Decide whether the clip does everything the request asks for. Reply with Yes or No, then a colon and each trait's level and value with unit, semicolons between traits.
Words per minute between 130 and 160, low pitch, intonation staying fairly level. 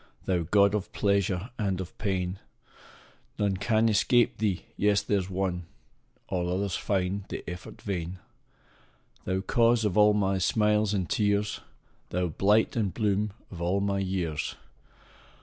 Yes: average, 150 wpm; low, 100 Hz; narrow, 2.3 semitones